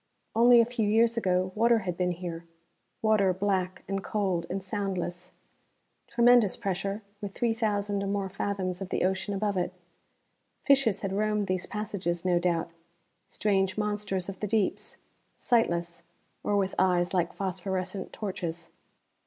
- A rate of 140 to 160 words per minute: Yes, average, 145 wpm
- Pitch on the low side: No, high, 195 Hz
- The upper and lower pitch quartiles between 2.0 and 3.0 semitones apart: Yes, narrow, 2.5 semitones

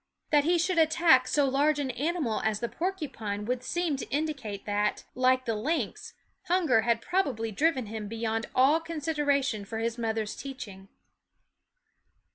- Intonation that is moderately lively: No, wide, 5.8 semitones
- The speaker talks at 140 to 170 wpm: Yes, average, 150 wpm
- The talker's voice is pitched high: Yes, very high, 260 Hz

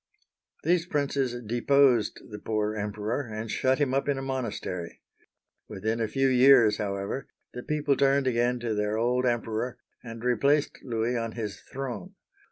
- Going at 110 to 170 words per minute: Yes, average, 155 wpm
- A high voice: No, low, 120 Hz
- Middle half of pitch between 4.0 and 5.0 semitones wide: No, average, 3.6 semitones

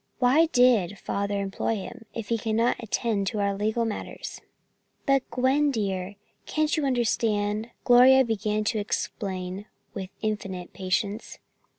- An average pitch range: Yes, average, 3.3 semitones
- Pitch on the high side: Yes, high, 215 Hz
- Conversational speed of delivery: No, slow, 130 wpm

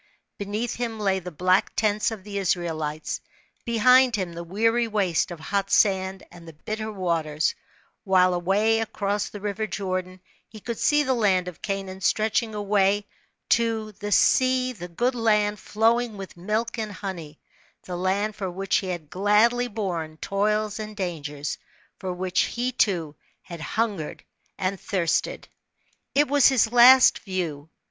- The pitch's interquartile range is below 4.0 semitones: Yes, average, 3.4 semitones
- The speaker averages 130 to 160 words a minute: Yes, average, 155 wpm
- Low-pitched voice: No, high, 200 Hz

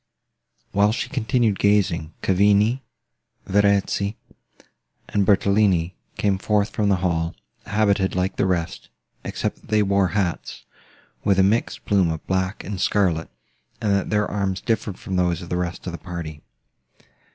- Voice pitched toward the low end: Yes, low, 100 Hz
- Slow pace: No, average, 150 wpm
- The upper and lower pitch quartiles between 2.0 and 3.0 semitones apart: Yes, narrow, 2.4 semitones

